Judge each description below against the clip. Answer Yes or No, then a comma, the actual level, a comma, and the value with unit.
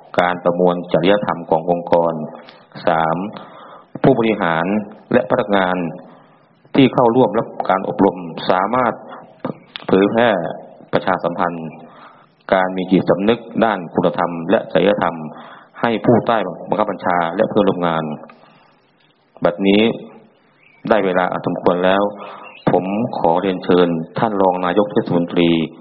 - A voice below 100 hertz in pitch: Yes, very low, 90 Hz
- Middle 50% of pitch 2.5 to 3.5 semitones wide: Yes, average, 3.0 semitones